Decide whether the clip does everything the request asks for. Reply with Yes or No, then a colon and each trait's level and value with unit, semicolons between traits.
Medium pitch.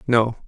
No: low, 120 Hz